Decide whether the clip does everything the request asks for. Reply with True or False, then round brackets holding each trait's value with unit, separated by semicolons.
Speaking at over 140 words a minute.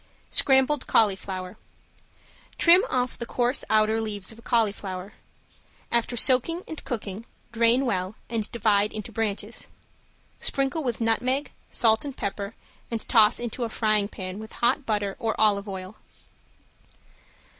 False (135 wpm)